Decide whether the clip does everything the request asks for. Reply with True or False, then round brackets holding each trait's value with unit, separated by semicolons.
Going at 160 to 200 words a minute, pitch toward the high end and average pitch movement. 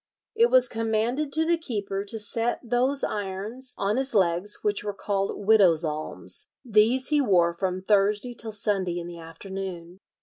True (165 wpm; 205 Hz; 4.4 semitones)